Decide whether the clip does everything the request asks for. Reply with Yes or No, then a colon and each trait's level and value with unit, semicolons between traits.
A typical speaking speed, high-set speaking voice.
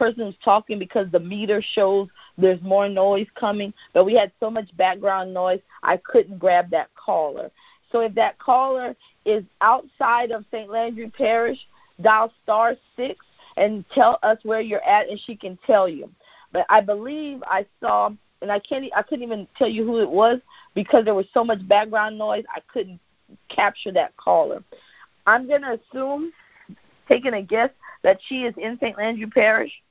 Yes: average, 180 wpm; high, 220 Hz